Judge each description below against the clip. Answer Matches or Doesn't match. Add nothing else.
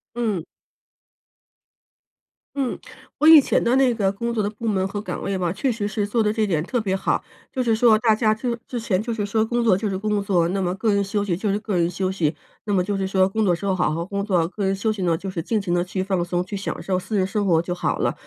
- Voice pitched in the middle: Doesn't match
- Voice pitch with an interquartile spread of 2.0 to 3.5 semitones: Matches